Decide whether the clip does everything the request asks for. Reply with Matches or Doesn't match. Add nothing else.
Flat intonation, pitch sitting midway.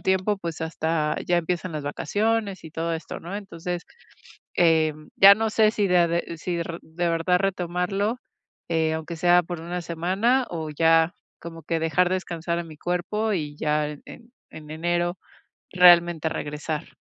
Matches